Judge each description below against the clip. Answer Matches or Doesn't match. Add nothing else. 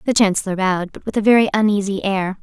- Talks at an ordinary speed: Doesn't match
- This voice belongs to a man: Doesn't match